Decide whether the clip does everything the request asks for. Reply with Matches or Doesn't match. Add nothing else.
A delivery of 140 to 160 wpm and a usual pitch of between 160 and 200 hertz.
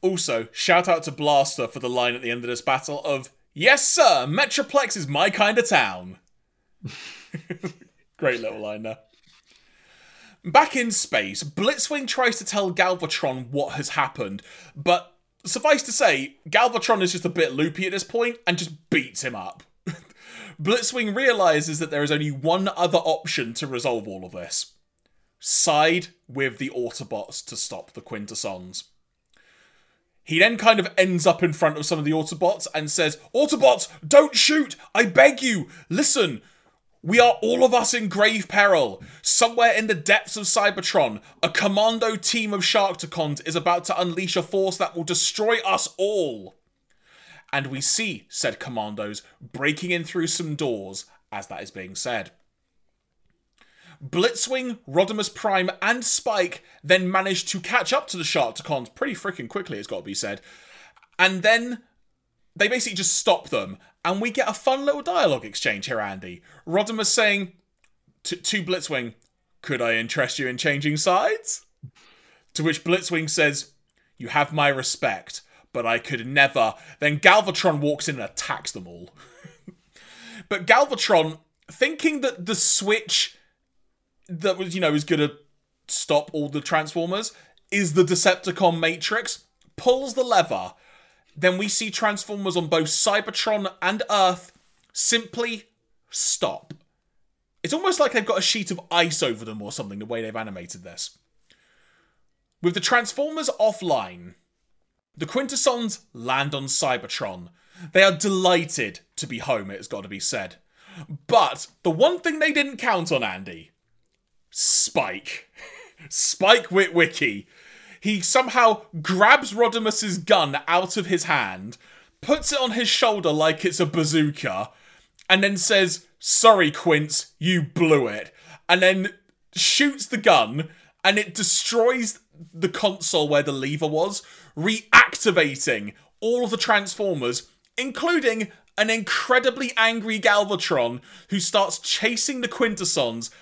Matches